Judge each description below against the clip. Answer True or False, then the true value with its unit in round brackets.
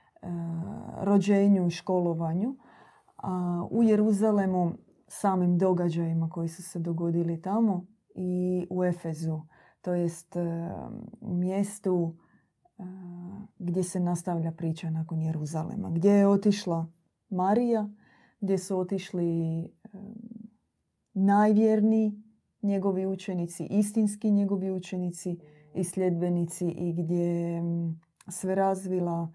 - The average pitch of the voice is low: False (185 Hz)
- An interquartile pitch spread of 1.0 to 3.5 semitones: True (2.9 semitones)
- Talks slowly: True (90 wpm)